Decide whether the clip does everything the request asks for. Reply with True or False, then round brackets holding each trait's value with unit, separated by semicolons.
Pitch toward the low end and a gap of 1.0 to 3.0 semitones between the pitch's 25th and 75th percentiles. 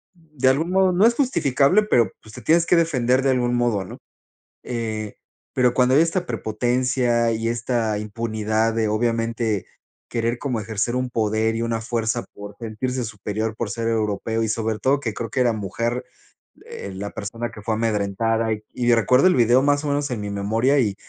True (115 Hz; 2.7 semitones)